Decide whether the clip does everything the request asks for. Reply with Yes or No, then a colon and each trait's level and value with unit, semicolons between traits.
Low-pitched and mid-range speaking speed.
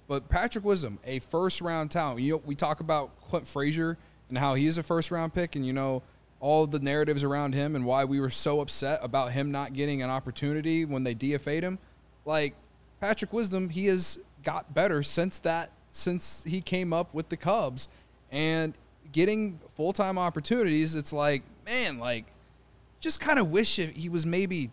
No: medium, 155 Hz; average, 180 wpm